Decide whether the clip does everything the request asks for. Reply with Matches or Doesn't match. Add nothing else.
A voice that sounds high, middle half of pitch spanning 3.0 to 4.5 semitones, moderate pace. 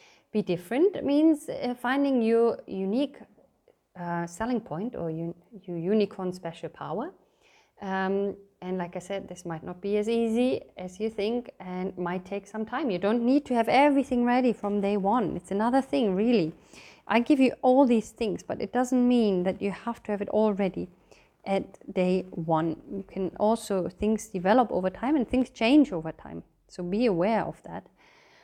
Doesn't match